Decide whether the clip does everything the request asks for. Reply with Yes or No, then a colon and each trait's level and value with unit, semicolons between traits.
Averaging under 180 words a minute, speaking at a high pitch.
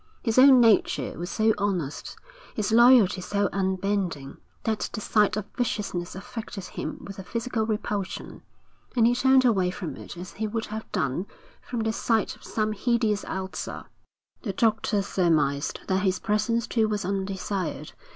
Yes: average, 160 wpm; high, 210 Hz